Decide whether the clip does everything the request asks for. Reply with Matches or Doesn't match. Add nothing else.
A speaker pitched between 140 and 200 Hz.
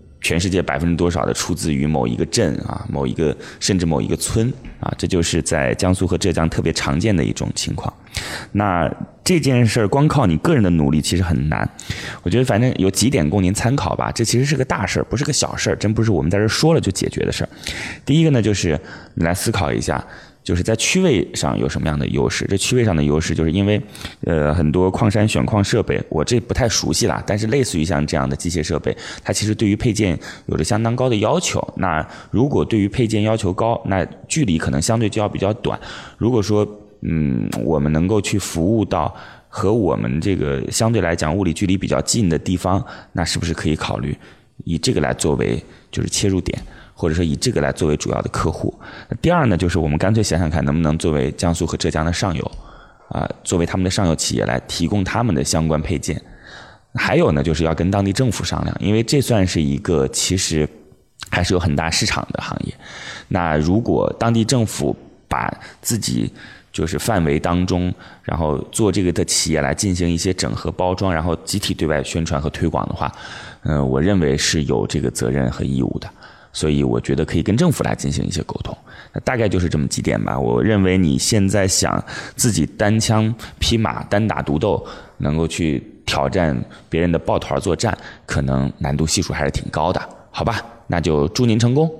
Doesn't match